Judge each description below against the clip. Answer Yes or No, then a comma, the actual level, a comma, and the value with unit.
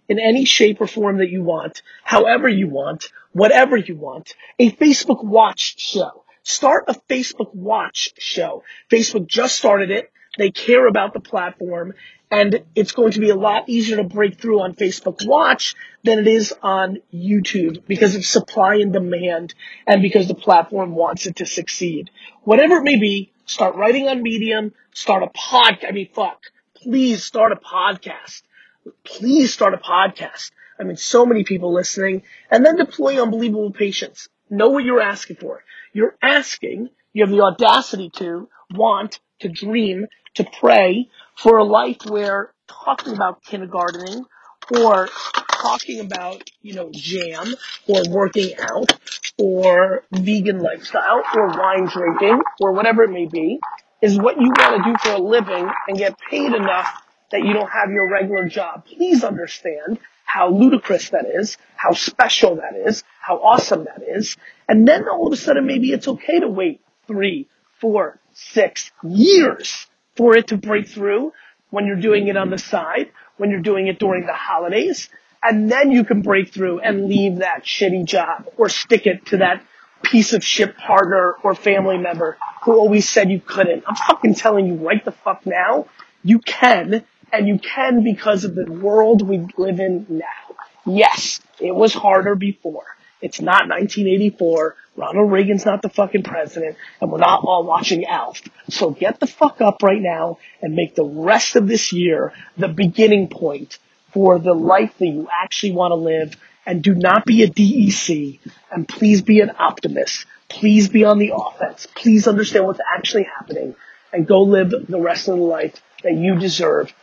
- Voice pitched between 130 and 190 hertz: No, high, 205 Hz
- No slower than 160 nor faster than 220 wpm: Yes, average, 170 wpm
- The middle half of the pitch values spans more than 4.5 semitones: No, average, 3.2 semitones